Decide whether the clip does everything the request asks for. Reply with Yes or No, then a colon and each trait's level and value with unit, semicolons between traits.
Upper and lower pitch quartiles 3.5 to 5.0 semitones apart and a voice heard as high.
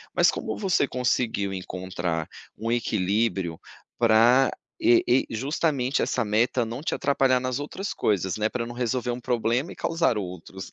No: average, 3.8 semitones; low, 120 Hz